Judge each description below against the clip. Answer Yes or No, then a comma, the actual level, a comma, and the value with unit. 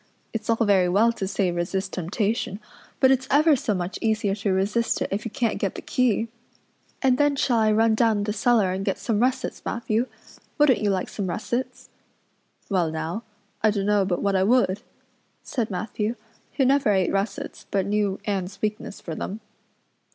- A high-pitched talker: Yes, high, 210 Hz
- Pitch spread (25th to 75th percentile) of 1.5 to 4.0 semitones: Yes, average, 3.2 semitones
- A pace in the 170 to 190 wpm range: Yes, average, 180 wpm